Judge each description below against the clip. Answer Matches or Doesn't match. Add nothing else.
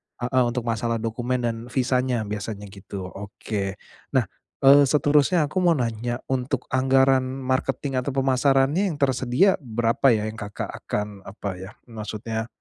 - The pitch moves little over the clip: Doesn't match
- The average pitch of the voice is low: Matches